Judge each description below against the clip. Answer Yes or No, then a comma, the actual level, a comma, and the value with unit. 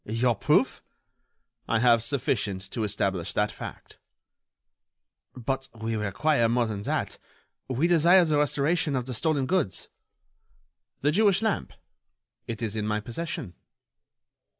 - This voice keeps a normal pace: No, slow, 125 wpm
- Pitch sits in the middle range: No, low, 120 Hz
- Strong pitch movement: Yes, wide, 5.8 semitones